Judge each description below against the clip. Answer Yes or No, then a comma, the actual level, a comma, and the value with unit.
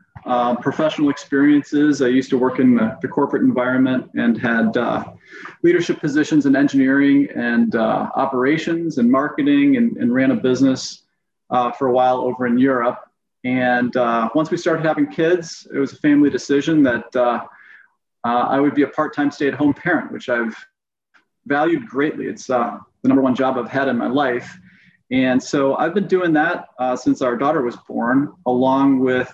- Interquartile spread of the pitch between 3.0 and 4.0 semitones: No, average, 4.8 semitones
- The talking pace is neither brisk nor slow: Yes, average, 185 wpm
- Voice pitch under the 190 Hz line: Yes, medium, 140 Hz